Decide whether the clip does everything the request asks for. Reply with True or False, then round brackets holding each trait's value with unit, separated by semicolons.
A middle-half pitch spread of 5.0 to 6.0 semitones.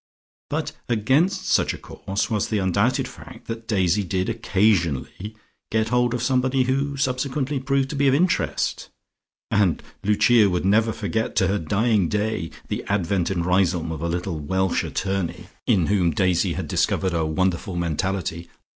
True (5.3 semitones)